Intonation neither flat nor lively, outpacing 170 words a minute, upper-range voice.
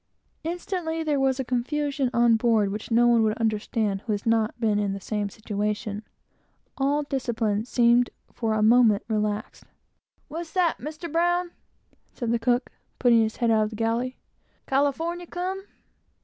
No: average, 5.0 semitones; average, 165 wpm; high, 235 Hz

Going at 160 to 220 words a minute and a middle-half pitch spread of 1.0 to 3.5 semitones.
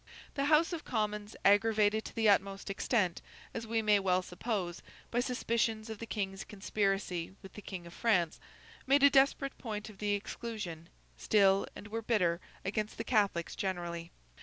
Yes: average, 165 wpm; average, 2.9 semitones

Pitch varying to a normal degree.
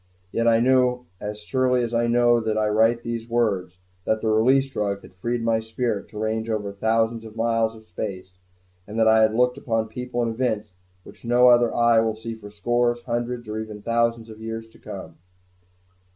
No: narrow, 1.6 semitones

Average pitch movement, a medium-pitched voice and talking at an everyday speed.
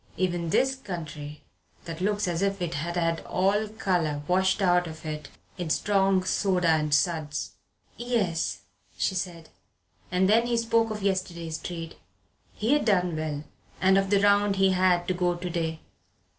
Yes: average, 3.1 semitones; medium, 180 Hz; average, 170 wpm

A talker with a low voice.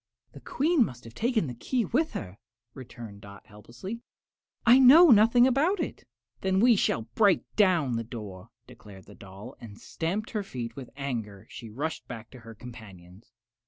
Yes: low, 125 Hz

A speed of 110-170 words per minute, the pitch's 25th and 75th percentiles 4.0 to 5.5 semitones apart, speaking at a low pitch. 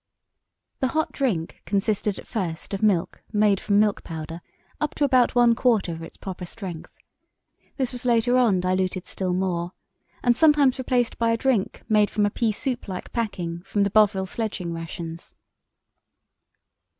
No: average, 160 wpm; average, 4.7 semitones; high, 205 Hz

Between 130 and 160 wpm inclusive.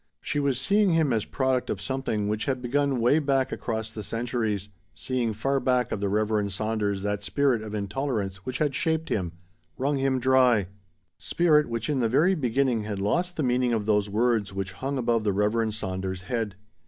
No: average, 190 wpm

